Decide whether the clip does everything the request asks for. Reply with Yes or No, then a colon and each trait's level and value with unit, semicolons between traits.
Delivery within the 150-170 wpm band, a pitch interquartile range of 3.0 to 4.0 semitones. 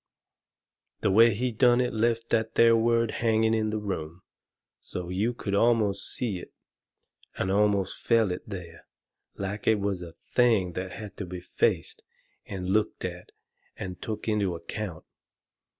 Yes: average, 155 wpm; average, 3.7 semitones